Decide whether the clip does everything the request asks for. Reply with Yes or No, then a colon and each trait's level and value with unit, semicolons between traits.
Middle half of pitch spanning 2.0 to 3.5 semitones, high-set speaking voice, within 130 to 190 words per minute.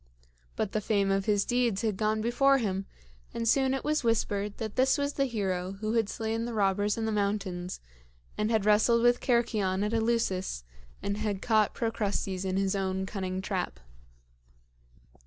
Yes: average, 2.9 semitones; high, 210 Hz; average, 175 wpm